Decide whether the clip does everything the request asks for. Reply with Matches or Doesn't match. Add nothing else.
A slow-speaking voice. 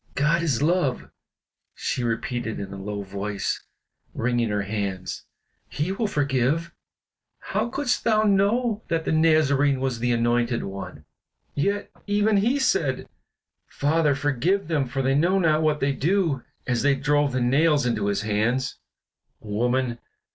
Doesn't match